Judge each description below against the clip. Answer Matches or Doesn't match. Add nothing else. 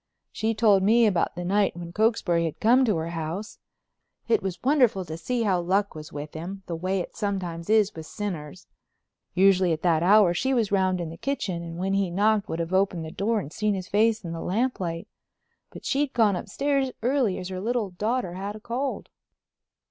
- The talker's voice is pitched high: Matches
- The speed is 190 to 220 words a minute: Matches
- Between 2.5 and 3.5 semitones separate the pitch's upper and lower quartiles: Doesn't match